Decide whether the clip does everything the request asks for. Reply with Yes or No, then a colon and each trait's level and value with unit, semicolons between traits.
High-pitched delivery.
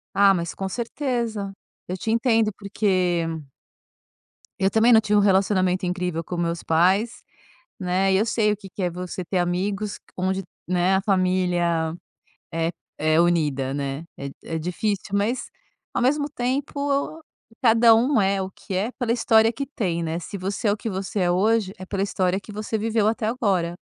Yes: high, 195 Hz